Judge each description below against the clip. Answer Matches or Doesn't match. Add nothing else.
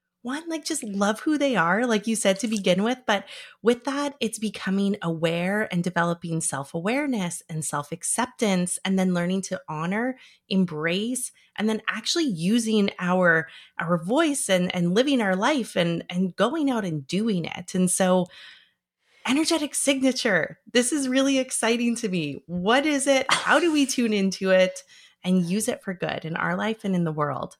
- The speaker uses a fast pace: Doesn't match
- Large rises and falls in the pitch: Matches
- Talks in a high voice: Matches